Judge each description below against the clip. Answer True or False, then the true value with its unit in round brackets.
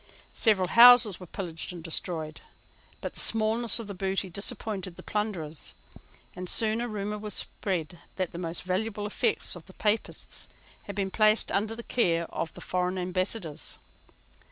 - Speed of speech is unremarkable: True (160 wpm)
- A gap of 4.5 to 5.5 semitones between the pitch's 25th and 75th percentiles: False (3.3 semitones)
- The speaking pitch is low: False (195 Hz)